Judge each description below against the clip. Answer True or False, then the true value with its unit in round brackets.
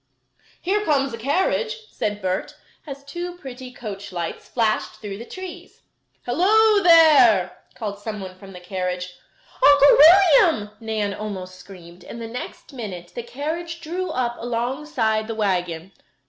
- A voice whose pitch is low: False (235 Hz)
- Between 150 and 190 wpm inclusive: False (140 wpm)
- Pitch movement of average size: False (7.7 semitones)